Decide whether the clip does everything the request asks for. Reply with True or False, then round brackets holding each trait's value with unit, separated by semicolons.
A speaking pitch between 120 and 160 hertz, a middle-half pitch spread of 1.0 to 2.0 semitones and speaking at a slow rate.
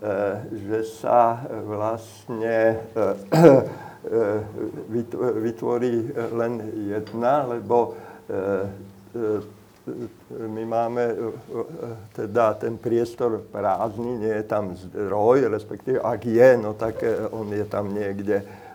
False (110 Hz; 1.7 semitones; 85 wpm)